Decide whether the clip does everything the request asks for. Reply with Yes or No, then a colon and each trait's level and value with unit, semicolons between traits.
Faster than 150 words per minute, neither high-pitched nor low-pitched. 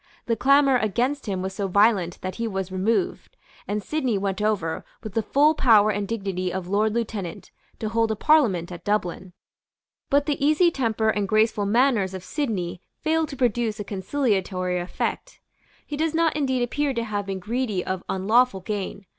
No: average, 180 wpm; high, 215 Hz